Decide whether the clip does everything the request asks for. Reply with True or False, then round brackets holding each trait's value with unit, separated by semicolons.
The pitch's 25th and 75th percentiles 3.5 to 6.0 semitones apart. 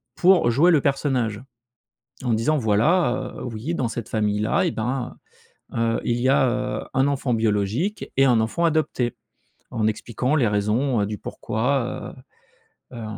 True (4.1 semitones)